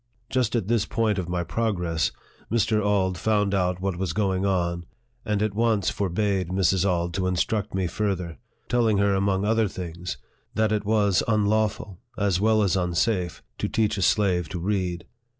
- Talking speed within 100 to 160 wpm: No, average, 170 wpm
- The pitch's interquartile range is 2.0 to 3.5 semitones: Yes, average, 3.0 semitones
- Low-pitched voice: Yes, low, 100 Hz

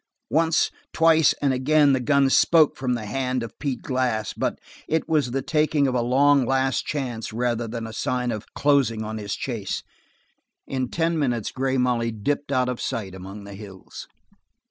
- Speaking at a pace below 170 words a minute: No, average, 180 wpm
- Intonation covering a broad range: No, average, 3.7 semitones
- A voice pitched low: Yes, low, 125 Hz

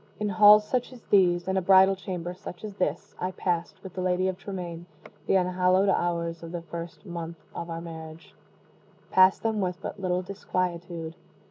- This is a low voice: No, medium, 180 Hz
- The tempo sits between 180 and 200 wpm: Yes, average, 185 wpm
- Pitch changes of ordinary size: No, narrow, 2.0 semitones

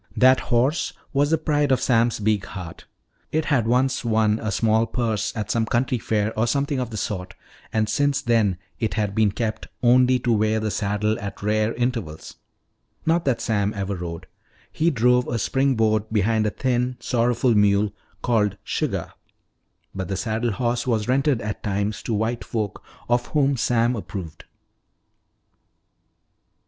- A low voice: Yes, low, 115 Hz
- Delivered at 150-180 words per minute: Yes, average, 160 wpm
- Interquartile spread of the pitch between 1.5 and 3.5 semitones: Yes, average, 2.9 semitones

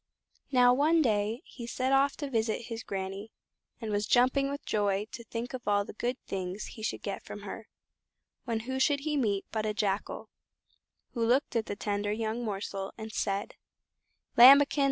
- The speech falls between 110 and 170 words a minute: No, average, 180 wpm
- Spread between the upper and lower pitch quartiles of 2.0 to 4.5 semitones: Yes, average, 3.8 semitones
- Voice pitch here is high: Yes, high, 225 Hz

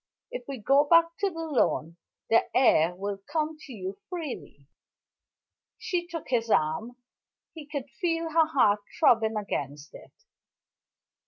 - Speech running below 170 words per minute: Yes, average, 140 wpm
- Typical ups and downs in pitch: No, wide, 8.2 semitones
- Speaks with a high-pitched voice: Yes, very high, 255 Hz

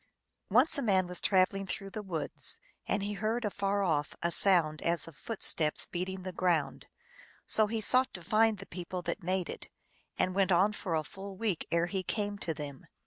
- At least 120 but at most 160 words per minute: No, average, 195 wpm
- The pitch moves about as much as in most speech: Yes, average, 3.1 semitones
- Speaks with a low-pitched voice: No, high, 190 Hz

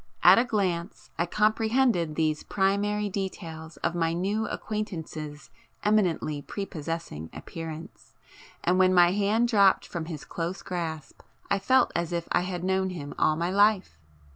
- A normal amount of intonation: Yes, average, 3.8 semitones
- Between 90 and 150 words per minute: Yes, average, 145 wpm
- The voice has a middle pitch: Yes, medium, 180 Hz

